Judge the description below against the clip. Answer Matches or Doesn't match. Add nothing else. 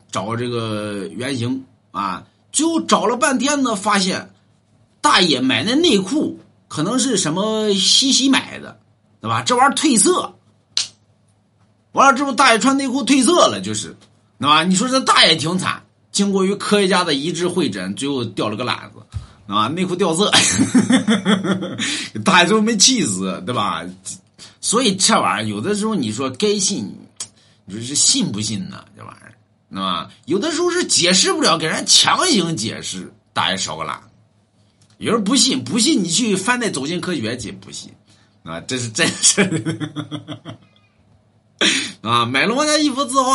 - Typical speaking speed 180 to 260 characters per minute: Matches